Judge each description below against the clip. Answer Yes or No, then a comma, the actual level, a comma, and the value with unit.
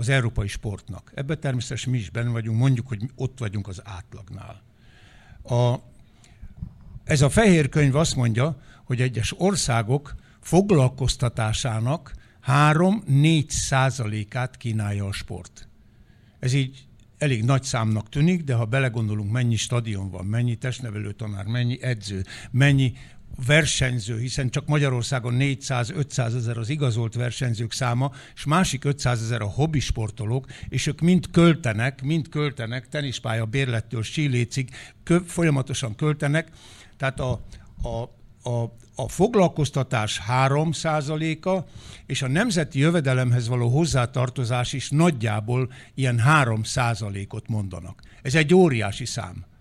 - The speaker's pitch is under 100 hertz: No, low, 125 Hz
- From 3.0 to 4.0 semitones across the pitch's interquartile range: Yes, average, 3.7 semitones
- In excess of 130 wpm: No, average, 120 wpm